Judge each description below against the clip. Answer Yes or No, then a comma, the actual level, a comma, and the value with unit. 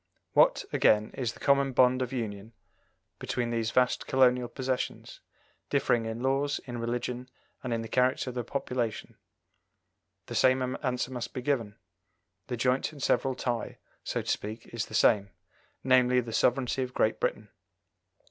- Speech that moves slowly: No, average, 155 wpm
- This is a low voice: Yes, low, 125 Hz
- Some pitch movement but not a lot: No, narrow, 1.9 semitones